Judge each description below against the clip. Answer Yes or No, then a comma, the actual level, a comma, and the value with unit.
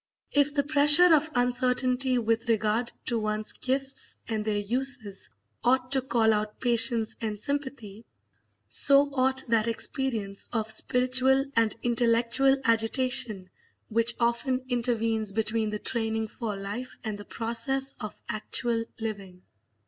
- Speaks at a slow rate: Yes, slow, 130 wpm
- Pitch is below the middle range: No, high, 235 Hz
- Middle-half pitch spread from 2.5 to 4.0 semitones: Yes, average, 3.1 semitones